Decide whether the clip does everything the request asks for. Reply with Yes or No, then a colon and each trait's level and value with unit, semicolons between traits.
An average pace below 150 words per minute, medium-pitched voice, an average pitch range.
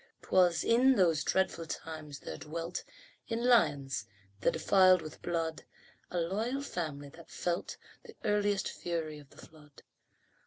Yes: average, 140 wpm; medium, 170 Hz; average, 4.3 semitones